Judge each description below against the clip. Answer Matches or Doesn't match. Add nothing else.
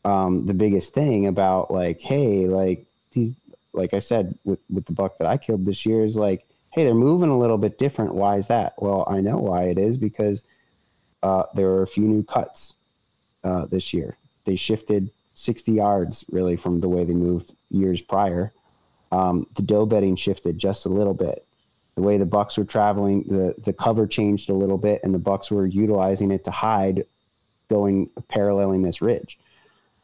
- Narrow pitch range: Matches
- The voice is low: Matches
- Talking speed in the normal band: Matches